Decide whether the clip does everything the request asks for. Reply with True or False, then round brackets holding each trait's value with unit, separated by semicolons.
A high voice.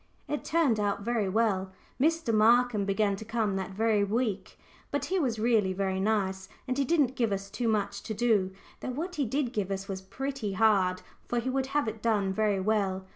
True (215 Hz)